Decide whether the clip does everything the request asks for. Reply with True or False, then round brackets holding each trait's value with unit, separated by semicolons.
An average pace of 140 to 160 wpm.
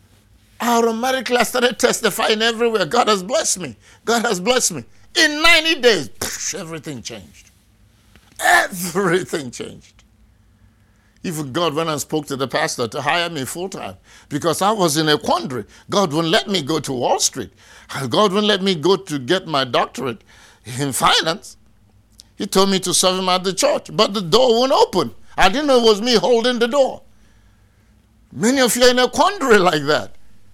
False (180 wpm)